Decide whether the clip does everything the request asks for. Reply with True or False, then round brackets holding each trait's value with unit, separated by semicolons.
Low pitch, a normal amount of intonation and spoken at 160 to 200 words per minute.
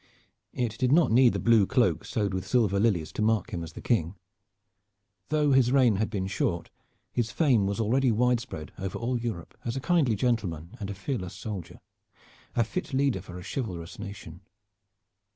True (110 Hz; 4.7 semitones; 180 wpm)